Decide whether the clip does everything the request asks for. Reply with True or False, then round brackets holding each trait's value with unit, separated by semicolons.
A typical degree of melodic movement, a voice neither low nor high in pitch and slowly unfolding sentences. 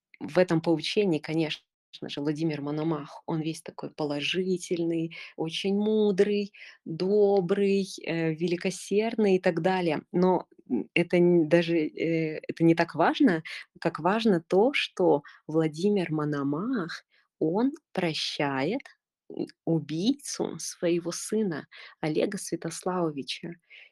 True (3.5 semitones; 170 Hz; 95 wpm)